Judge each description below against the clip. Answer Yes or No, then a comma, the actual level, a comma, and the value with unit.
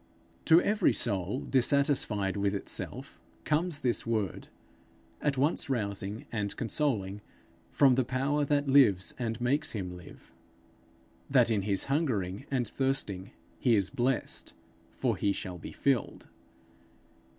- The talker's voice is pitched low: Yes, low, 120 Hz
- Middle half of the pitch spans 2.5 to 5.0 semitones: No, wide, 5.6 semitones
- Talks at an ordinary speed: No, slow, 130 wpm